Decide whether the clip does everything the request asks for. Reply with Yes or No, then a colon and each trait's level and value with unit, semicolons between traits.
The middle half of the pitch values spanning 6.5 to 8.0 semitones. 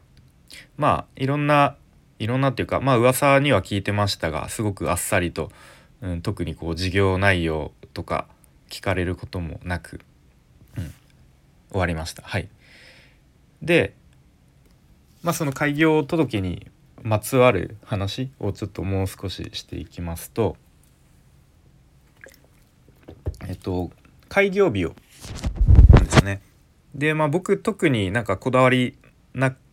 Yes: wide, 7.1 semitones